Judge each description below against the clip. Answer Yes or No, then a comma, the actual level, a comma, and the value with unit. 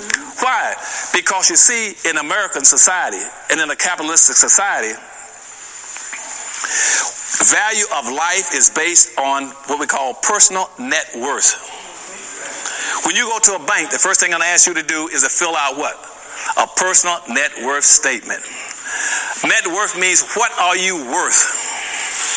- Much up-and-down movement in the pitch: No, average, 4.7 semitones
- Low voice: No, medium, 180 Hz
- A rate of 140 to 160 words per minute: Yes, average, 155 wpm